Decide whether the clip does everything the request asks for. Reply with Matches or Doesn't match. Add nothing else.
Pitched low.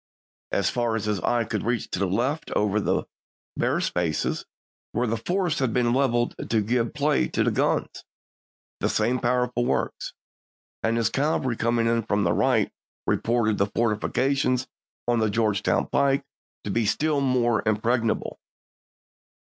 Matches